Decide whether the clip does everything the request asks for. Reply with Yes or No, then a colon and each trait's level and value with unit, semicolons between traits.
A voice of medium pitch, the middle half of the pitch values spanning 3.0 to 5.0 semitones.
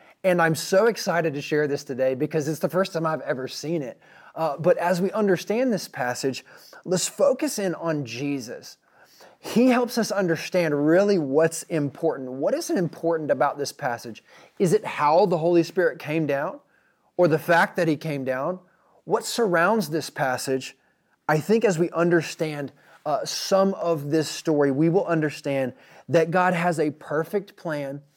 Yes: medium, 165 Hz; average, 4.3 semitones